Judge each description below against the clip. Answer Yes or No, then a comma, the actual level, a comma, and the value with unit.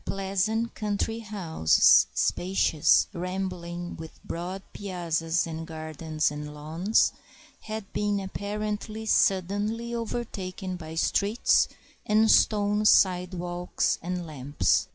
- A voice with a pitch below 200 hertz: Yes, medium, 185 Hz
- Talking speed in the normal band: No, slow, 95 wpm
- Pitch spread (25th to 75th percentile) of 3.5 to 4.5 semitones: Yes, average, 3.9 semitones